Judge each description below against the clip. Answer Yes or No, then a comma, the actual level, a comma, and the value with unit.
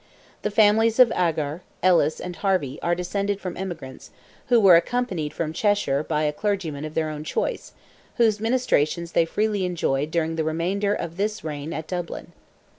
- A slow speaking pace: No, average, 170 wpm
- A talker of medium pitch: Yes, medium, 175 Hz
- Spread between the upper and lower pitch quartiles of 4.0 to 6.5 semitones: Yes, average, 4.7 semitones